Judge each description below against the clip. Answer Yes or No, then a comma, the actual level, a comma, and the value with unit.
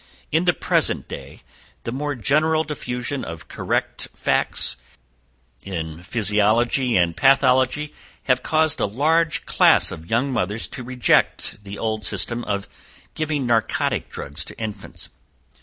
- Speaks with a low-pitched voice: Yes, low, 120 Hz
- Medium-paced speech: No, slow, 130 wpm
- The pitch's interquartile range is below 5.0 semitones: No, wide, 5.5 semitones